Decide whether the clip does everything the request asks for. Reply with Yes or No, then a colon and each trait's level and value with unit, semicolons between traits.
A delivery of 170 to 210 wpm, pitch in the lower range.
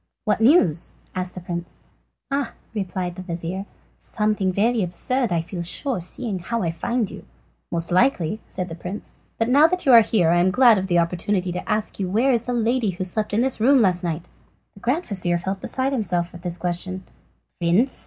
No: average, 200 wpm; high, 190 Hz